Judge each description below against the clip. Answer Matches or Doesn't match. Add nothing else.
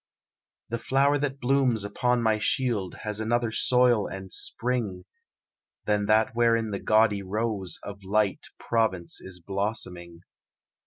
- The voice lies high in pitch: Doesn't match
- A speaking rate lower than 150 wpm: Matches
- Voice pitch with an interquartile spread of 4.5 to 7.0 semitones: Doesn't match